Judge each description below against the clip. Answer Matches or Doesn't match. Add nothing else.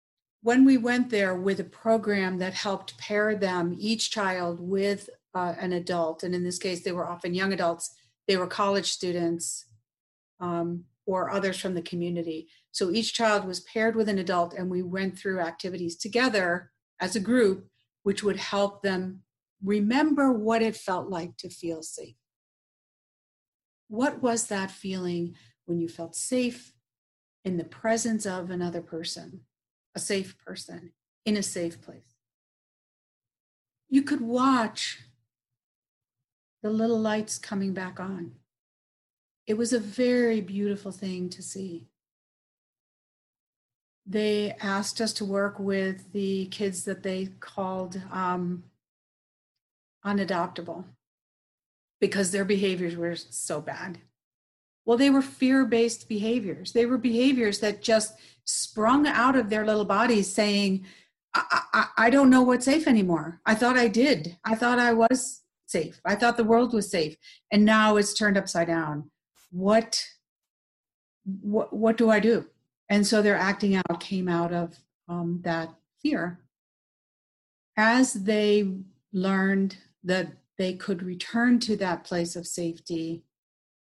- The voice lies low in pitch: Doesn't match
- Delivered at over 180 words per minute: Doesn't match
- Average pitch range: Matches